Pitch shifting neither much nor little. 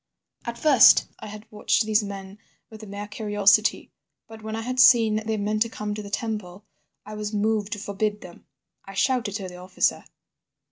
No: narrow, 1.4 semitones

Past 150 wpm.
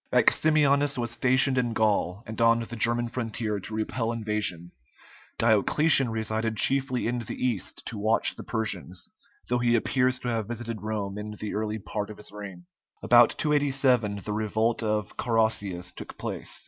Yes: average, 160 wpm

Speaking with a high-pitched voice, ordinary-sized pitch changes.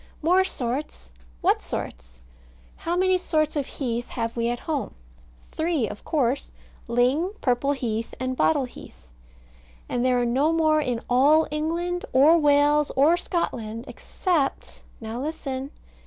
Yes: very high, 275 Hz; average, 4.7 semitones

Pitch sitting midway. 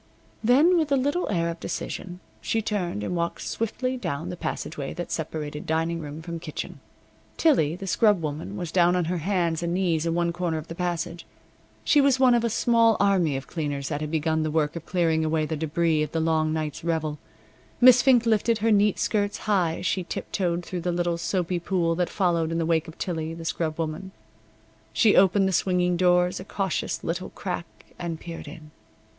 Yes: medium, 170 Hz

